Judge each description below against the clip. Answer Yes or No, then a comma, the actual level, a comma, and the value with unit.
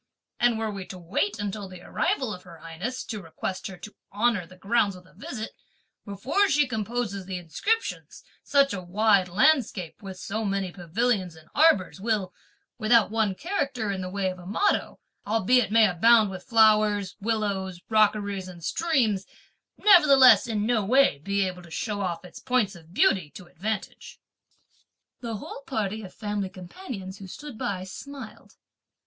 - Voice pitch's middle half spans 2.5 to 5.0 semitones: Yes, average, 3.7 semitones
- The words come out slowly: No, average, 165 wpm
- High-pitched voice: Yes, high, 205 Hz